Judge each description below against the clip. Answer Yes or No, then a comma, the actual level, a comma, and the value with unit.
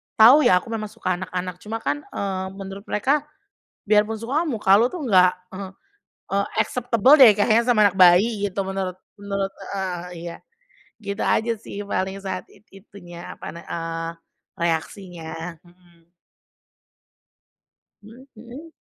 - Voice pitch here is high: Yes, high, 200 Hz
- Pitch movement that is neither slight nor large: Yes, average, 3.6 semitones